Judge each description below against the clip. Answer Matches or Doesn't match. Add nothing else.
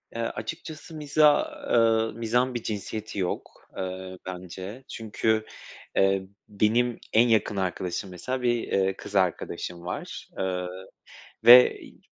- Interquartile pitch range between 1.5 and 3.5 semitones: Doesn't match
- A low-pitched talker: Matches